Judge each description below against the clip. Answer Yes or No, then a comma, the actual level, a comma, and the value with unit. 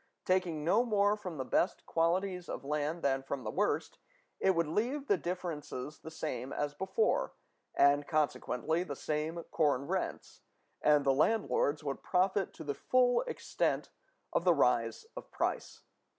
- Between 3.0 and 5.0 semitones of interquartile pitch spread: Yes, average, 4.7 semitones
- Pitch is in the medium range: Yes, medium, 160 Hz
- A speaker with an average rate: Yes, average, 155 wpm